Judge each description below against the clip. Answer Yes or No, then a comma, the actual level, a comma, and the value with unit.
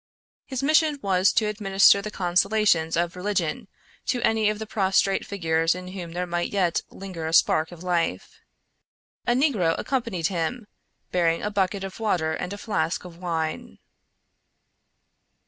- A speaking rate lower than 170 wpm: Yes, average, 150 wpm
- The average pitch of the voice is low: No, medium, 185 Hz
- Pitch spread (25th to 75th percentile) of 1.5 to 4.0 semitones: Yes, average, 3.6 semitones